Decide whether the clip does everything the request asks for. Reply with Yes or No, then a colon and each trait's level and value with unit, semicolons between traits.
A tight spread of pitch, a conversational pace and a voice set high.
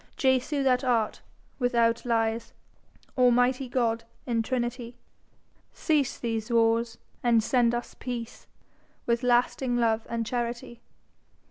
No: narrow, 1.4 semitones; slow, 110 wpm; high, 240 Hz